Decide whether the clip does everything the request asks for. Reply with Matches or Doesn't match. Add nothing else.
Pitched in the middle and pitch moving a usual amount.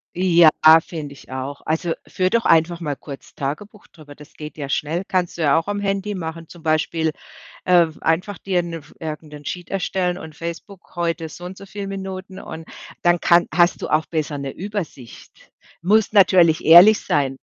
Matches